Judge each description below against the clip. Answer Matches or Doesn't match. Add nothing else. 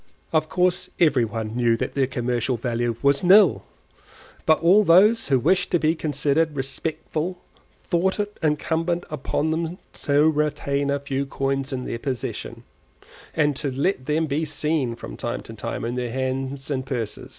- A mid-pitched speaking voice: Matches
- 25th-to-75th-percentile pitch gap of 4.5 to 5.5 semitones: Doesn't match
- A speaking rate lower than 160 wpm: Doesn't match